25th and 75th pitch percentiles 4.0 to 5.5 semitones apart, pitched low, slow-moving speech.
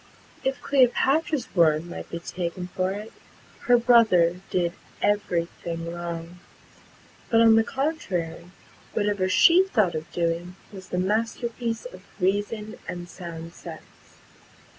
No: average, 4.9 semitones; medium, 185 Hz; slow, 125 wpm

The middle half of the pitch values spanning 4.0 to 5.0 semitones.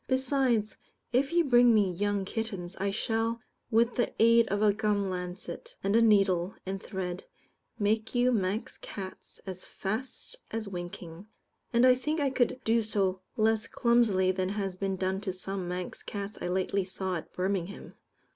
No: average, 3.6 semitones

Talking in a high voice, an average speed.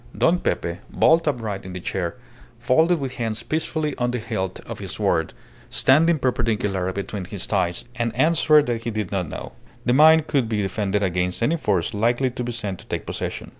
No: low, 115 Hz; average, 195 wpm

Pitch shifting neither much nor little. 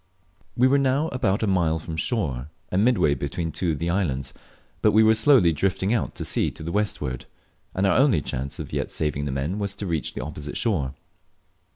No: wide, 6.6 semitones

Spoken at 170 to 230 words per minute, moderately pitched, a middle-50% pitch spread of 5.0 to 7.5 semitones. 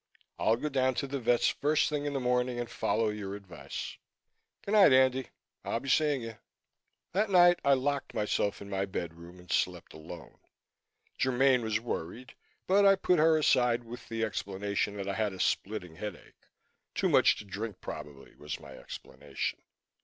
No: average, 175 wpm; low, 115 Hz; wide, 5.5 semitones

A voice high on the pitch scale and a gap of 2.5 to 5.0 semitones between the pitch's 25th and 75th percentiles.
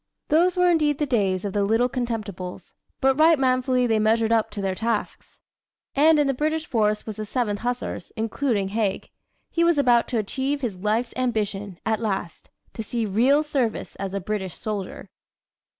Yes: high, 230 Hz; average, 4.4 semitones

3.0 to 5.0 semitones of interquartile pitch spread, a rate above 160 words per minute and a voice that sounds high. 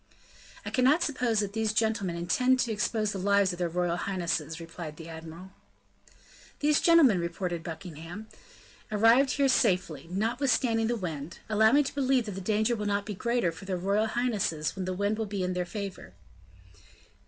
Yes: average, 4.5 semitones; average, 175 wpm; high, 200 Hz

